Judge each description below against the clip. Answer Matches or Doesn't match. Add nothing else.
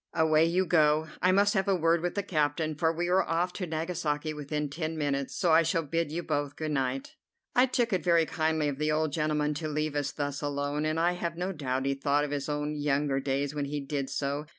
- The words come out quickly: Matches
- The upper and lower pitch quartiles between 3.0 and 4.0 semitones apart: Doesn't match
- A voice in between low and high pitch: Matches